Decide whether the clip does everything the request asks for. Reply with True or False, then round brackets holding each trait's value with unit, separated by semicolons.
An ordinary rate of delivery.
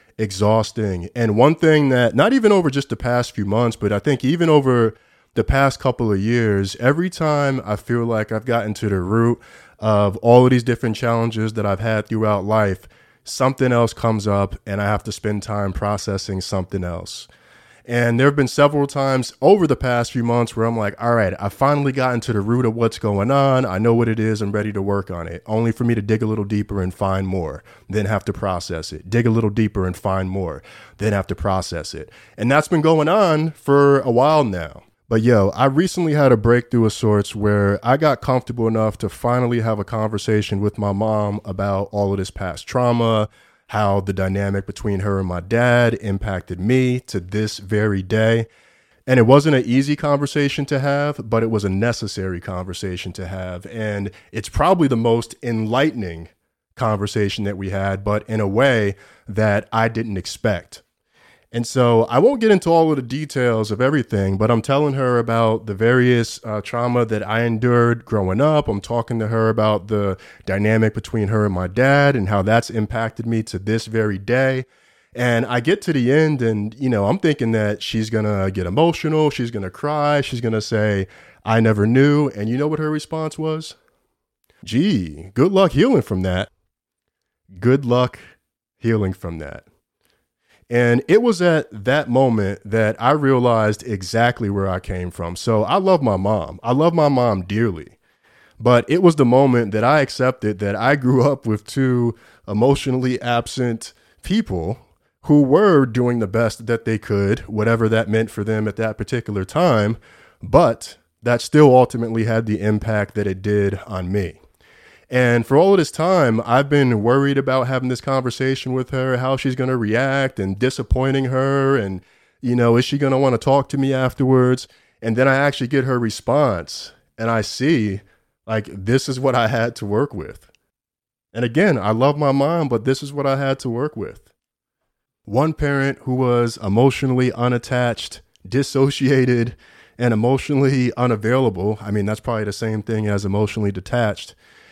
True (190 wpm)